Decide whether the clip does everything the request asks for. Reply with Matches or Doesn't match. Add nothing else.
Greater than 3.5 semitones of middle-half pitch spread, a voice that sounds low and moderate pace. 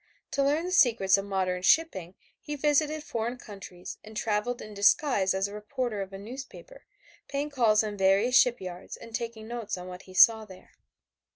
Doesn't match